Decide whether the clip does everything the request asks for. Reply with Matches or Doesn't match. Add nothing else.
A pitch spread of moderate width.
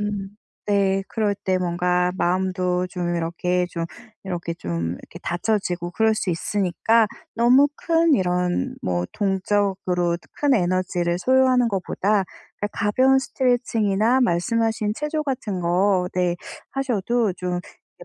Matches